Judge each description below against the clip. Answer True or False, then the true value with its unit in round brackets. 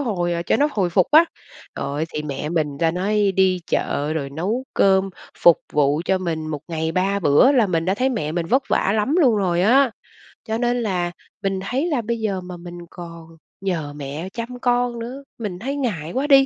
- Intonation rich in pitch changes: True (6.4 semitones)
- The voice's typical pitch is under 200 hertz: True (190 Hz)